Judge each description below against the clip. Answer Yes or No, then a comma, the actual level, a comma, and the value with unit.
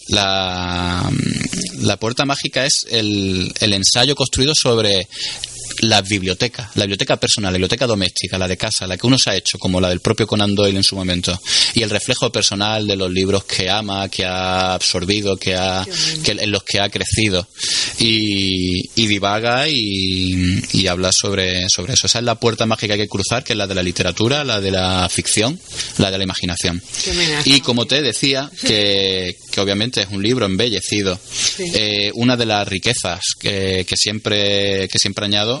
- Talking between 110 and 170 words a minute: No, average, 185 wpm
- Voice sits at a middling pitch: No, low, 100 Hz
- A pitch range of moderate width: Yes, average, 3.8 semitones